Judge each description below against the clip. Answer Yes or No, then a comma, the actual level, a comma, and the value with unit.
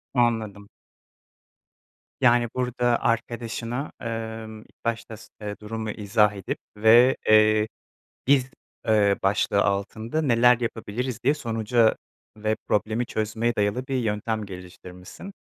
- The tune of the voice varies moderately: No, narrow, 2.2 semitones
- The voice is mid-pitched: No, low, 110 Hz